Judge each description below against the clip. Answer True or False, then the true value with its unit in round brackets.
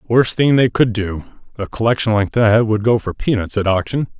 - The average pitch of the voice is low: True (110 Hz)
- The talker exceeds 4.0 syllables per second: True (5.1 syllables/s)